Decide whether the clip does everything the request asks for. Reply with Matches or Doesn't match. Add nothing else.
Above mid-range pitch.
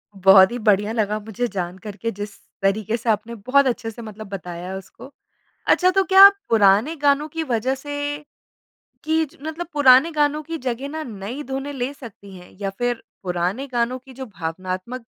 Matches